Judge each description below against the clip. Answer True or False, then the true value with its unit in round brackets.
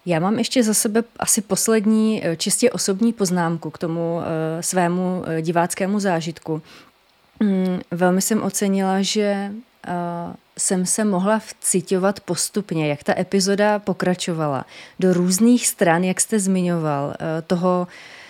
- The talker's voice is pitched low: False (185 Hz)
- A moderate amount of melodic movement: True (3.3 semitones)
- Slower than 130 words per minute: True (115 wpm)